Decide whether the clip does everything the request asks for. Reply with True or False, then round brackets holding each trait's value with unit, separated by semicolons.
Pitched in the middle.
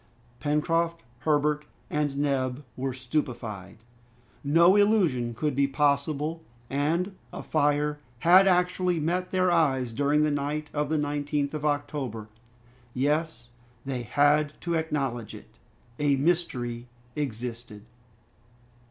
True (145 Hz)